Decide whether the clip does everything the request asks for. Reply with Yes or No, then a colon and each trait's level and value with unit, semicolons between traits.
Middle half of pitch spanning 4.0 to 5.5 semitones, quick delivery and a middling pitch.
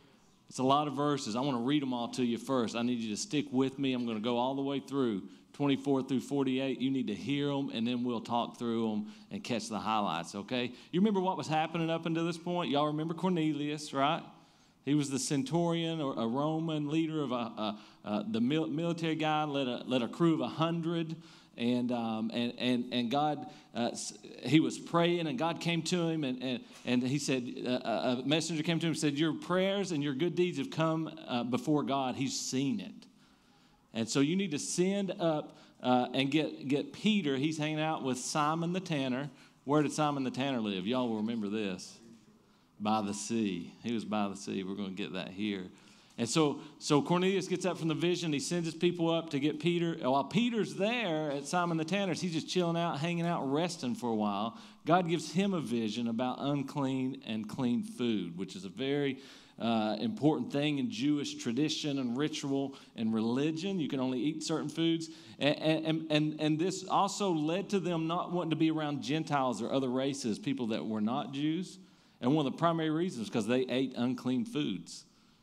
Yes: average, 4.8 semitones; fast, 215 wpm; medium, 145 Hz